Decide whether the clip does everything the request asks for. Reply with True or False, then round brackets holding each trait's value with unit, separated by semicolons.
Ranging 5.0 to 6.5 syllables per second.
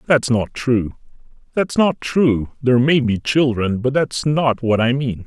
False (4.1 syllables/s)